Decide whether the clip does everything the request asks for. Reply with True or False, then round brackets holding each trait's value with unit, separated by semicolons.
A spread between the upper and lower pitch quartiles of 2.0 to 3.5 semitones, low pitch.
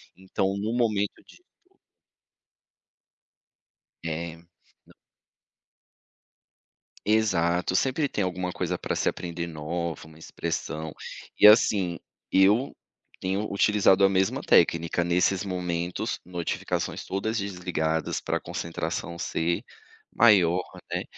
True (2.8 semitones; 90 Hz)